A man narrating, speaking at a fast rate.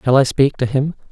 Yes: male; fast, 270 wpm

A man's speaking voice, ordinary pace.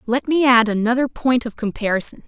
No: female; average, 185 wpm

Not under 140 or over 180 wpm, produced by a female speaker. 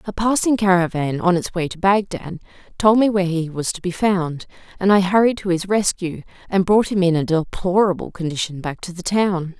No: fast, 205 wpm; female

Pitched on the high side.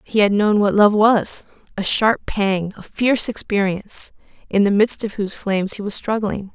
Yes: high, 205 Hz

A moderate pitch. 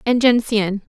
No: high, 220 Hz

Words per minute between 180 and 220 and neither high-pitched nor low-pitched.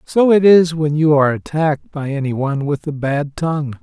Yes: fast, 205 wpm; medium, 150 Hz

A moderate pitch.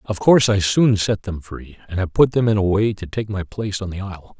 No: low, 100 Hz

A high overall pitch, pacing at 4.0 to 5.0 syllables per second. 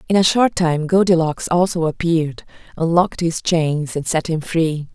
No: medium, 165 Hz; 4.8 syllables/s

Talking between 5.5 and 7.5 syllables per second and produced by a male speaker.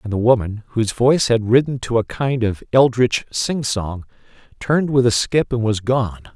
No: 5.0 syllables/s; male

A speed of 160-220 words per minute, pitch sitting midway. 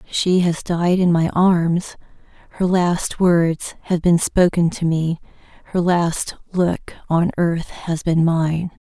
No: average, 150 wpm; medium, 170 Hz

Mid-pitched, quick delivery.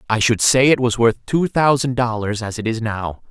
No: low, 120 Hz; fast, 235 wpm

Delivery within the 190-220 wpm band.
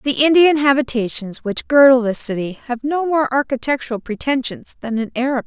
No: average, 175 wpm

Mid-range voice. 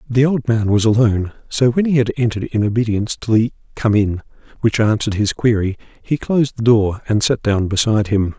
No: low, 115 Hz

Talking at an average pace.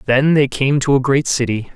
No: fast, 240 wpm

